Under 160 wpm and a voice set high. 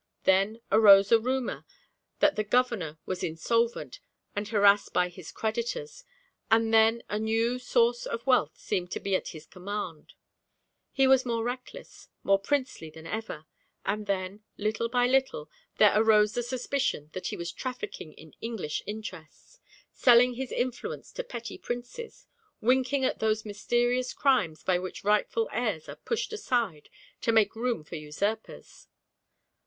Yes: average, 150 wpm; high, 220 Hz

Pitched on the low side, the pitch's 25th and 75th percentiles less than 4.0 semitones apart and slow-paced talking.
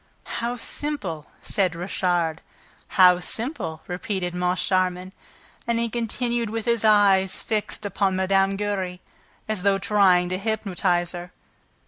No: high, 195 Hz; average, 3.2 semitones; slow, 120 wpm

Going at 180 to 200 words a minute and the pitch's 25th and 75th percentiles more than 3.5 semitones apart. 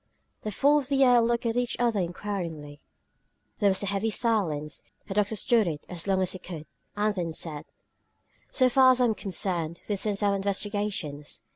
Yes: average, 185 wpm; average, 4.6 semitones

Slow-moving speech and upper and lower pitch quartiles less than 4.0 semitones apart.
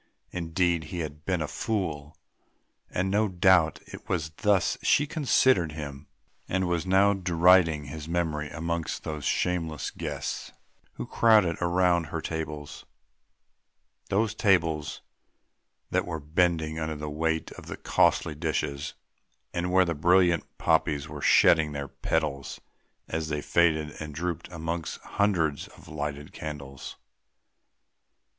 Yes: slow, 130 wpm; average, 2.9 semitones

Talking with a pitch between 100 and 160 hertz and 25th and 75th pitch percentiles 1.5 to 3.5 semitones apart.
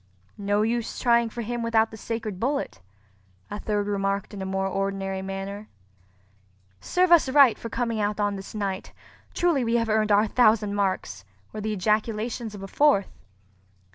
No: high, 215 Hz; average, 2.8 semitones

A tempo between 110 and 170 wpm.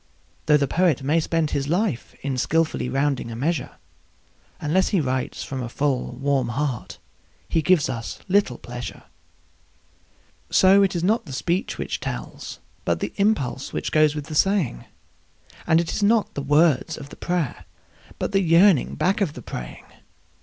Yes: average, 165 wpm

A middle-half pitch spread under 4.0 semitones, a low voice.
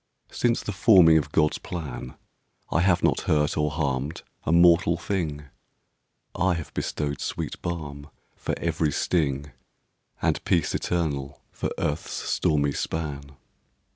Yes: average, 2.9 semitones; very low, 80 Hz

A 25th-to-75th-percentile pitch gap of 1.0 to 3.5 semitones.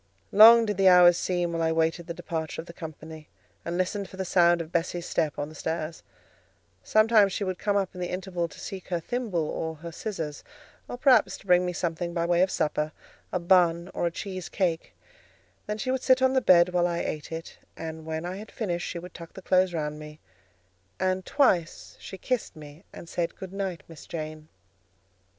Yes: average, 2.7 semitones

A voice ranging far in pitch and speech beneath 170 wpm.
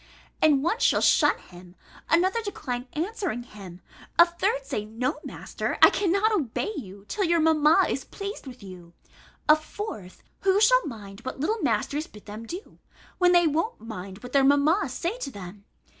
No: wide, 8.9 semitones; average, 175 wpm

